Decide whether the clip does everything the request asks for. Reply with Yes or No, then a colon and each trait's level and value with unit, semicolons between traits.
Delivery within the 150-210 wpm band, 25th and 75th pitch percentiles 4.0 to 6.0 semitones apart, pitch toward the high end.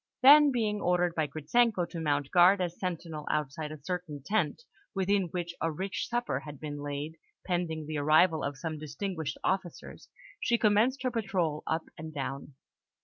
No: average, 165 wpm; average, 4.4 semitones; medium, 170 Hz